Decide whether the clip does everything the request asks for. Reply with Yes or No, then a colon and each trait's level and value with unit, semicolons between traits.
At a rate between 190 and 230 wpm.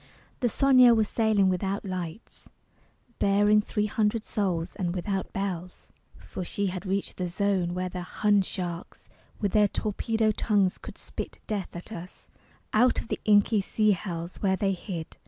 No: average, 160 wpm